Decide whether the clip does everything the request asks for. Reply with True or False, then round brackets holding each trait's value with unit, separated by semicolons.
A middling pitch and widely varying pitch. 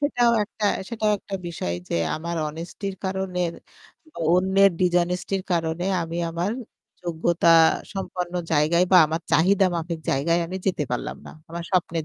False (175 Hz; 2.5 semitones)